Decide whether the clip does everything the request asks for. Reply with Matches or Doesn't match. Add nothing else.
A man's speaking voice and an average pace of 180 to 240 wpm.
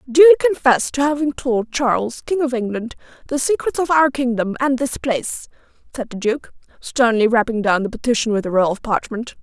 Doesn't match